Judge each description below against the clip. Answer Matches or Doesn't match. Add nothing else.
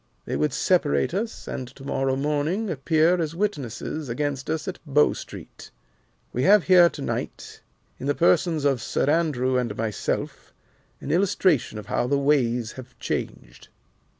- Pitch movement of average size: Matches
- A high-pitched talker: Doesn't match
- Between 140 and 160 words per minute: Matches